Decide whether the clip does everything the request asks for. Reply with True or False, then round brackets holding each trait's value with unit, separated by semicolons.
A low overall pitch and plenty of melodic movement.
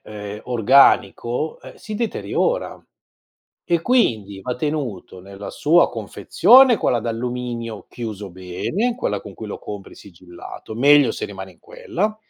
True (115 Hz; 7.6 semitones)